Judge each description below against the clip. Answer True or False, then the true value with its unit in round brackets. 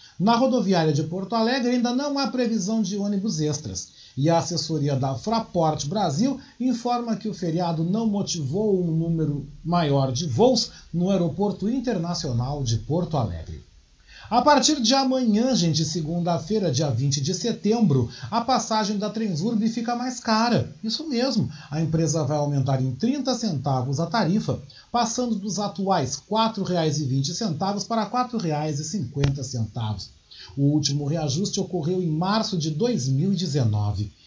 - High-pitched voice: False (180 Hz)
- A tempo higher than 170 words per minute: False (140 wpm)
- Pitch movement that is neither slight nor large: False (7.0 semitones)